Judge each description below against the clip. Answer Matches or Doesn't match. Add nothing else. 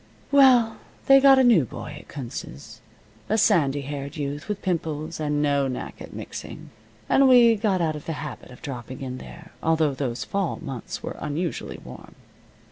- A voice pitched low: Doesn't match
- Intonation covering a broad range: Matches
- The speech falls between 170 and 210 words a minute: Matches